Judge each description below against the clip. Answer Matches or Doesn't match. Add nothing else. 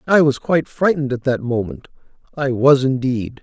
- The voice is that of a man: Matches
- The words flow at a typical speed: Matches